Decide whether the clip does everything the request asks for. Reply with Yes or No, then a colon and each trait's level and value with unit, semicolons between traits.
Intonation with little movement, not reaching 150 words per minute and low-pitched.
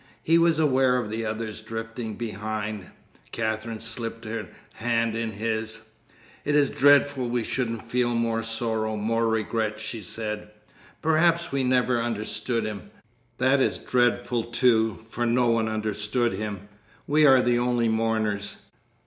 Yes: narrow, 2.1 semitones; average, 140 wpm; low, 115 Hz